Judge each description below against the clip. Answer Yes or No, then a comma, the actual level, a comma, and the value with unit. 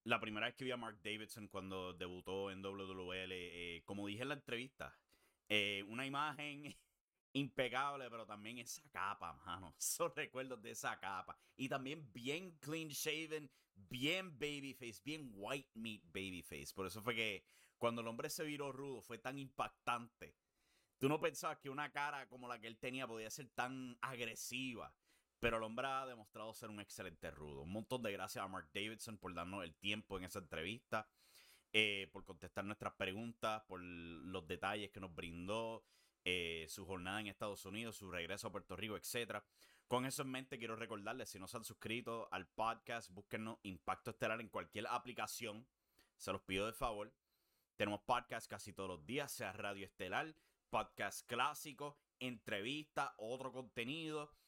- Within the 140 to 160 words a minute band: No, average, 170 wpm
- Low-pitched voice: Yes, low, 115 Hz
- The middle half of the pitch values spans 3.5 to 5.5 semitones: Yes, average, 4.9 semitones